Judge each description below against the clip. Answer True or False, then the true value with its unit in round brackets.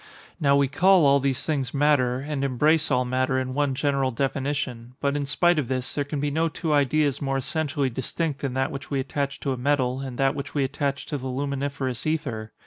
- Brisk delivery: True (220 wpm)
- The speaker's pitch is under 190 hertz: True (140 Hz)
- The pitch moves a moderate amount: False (1.9 semitones)